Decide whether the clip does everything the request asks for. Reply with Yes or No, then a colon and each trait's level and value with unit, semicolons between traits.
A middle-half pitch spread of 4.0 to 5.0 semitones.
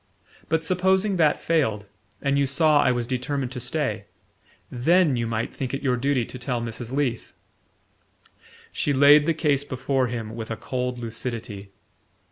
No: average, 3.6 semitones